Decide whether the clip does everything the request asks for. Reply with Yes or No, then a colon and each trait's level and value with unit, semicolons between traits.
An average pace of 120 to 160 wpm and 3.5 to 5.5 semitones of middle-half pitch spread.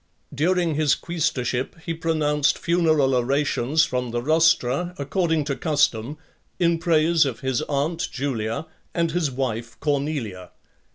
Yes: slow, 135 wpm; average, 3.9 semitones